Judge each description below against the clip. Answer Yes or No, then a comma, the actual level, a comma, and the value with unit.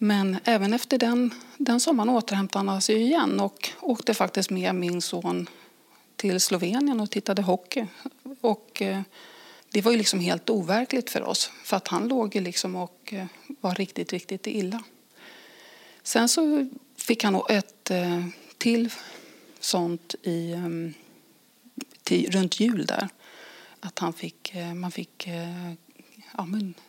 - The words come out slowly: Yes, slow, 130 wpm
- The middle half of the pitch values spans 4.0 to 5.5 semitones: Yes, average, 4.6 semitones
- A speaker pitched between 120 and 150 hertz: No, high, 205 Hz